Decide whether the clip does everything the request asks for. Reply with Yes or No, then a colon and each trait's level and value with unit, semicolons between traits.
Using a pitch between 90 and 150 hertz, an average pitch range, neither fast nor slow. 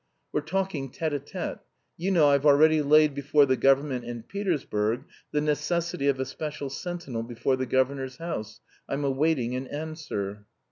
Yes: medium, 140 Hz; average, 3.2 semitones; average, 160 wpm